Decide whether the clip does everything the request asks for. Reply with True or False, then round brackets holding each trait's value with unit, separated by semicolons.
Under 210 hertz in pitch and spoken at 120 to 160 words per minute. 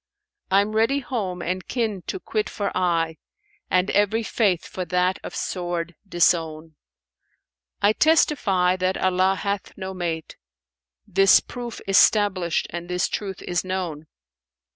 True (185 Hz; 140 wpm)